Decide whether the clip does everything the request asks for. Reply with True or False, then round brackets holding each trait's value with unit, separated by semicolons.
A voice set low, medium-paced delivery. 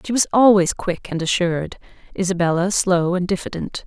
False (185 Hz; 155 wpm)